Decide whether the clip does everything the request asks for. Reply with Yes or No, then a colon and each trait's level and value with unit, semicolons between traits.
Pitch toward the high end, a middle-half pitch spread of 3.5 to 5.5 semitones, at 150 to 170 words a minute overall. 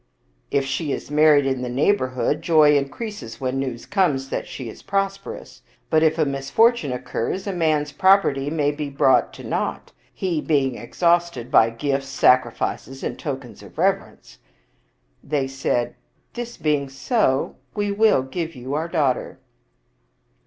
No: medium, 145 Hz; average, 4.2 semitones; average, 155 wpm